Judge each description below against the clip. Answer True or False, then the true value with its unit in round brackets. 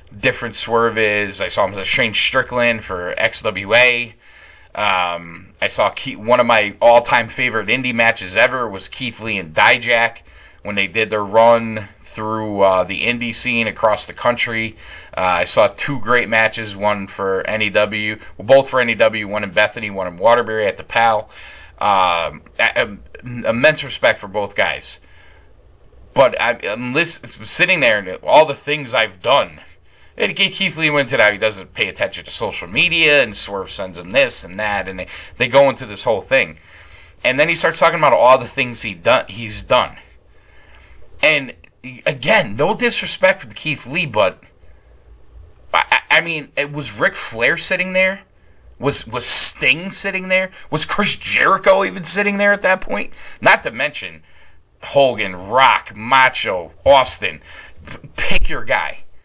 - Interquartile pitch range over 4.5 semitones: True (5.3 semitones)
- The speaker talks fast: False (170 wpm)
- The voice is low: True (115 Hz)